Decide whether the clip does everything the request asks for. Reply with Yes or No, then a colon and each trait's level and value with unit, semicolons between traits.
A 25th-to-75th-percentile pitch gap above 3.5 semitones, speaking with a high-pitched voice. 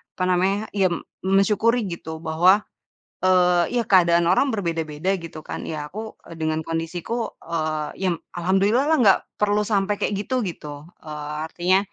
No: average, 4.1 semitones; medium, 180 Hz